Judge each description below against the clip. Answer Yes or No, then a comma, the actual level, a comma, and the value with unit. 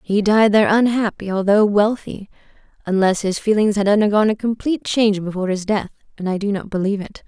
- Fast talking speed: No, average, 190 wpm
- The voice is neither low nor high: No, high, 205 Hz